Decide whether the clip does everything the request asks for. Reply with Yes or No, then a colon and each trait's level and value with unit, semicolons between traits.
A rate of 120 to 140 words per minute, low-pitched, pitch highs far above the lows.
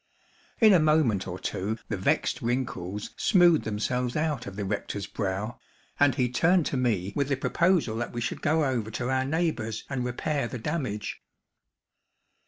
No: average, 170 wpm; low, 125 Hz; wide, 5.9 semitones